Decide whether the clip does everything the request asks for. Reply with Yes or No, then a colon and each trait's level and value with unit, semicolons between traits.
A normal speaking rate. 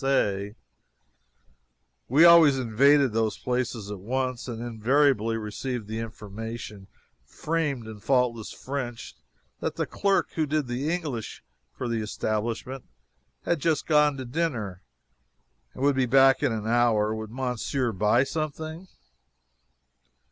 No: slow, 125 wpm